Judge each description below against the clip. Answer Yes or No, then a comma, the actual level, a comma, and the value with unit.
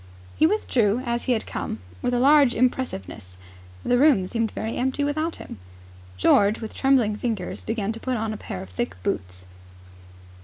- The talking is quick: No, average, 175 wpm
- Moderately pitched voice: No, high, 230 Hz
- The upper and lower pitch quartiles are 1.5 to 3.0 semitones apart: No, average, 4.4 semitones